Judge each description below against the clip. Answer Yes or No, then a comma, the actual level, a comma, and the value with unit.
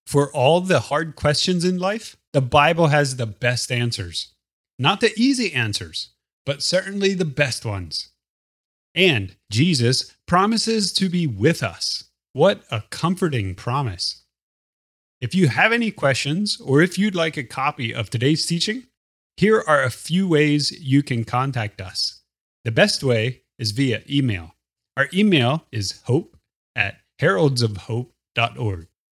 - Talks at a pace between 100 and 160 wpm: Yes, average, 140 wpm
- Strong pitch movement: Yes, wide, 7.2 semitones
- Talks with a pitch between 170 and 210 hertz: No, medium, 140 Hz